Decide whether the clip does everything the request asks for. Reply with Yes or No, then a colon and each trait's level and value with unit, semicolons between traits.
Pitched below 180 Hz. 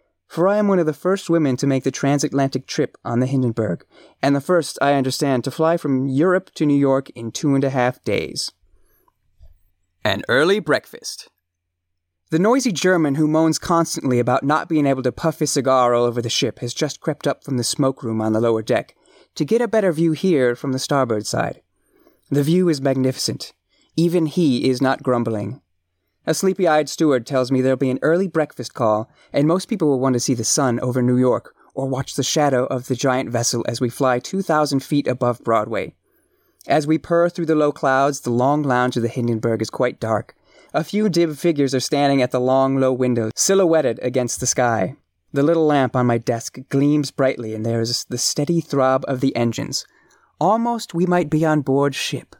Yes: low, 135 Hz